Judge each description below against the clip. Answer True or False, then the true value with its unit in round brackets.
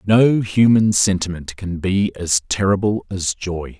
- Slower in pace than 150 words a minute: True (140 wpm)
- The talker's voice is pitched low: True (95 Hz)